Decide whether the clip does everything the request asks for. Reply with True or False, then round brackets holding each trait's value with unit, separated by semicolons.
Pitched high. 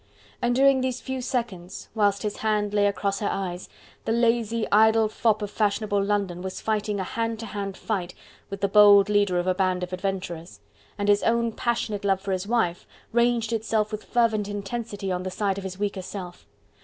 True (205 Hz)